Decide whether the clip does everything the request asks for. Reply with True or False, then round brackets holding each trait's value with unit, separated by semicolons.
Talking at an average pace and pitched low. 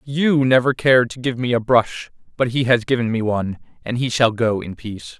False (230 wpm; 120 Hz)